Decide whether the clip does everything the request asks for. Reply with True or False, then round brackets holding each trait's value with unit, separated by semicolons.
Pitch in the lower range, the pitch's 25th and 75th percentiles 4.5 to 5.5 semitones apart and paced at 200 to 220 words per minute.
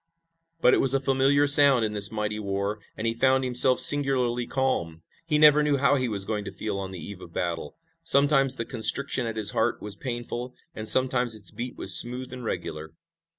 False (120 Hz; 4.1 semitones; 205 wpm)